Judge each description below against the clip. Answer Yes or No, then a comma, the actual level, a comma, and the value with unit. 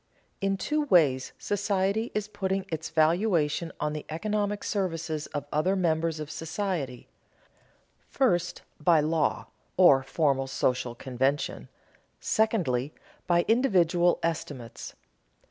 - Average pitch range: Yes, average, 4.8 semitones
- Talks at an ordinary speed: No, slow, 110 wpm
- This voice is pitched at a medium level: Yes, medium, 165 Hz